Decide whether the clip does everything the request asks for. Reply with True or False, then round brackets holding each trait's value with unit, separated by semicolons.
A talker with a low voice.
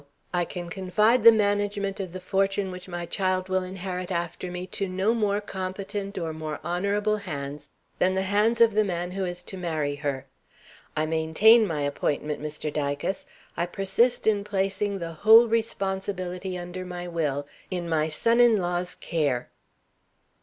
False (185 Hz)